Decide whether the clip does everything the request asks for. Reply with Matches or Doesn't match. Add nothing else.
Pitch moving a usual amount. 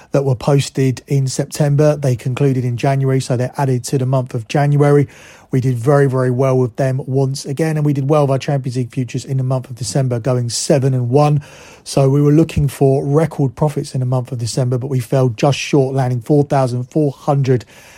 Doesn't match